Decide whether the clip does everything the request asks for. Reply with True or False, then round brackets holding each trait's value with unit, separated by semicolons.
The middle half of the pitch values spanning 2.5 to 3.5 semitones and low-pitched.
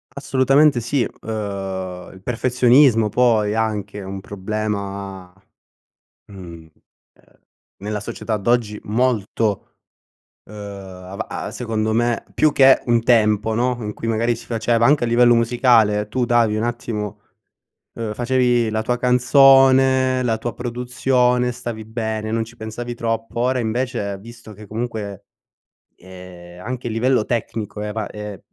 True (2.8 semitones; 115 Hz)